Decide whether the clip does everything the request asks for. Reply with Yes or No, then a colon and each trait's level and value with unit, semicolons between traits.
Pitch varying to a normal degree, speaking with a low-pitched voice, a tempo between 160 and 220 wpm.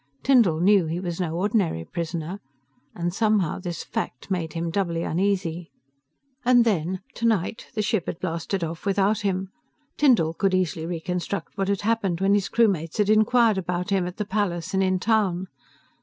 No: average, 3.3 semitones; medium, 185 Hz; average, 170 wpm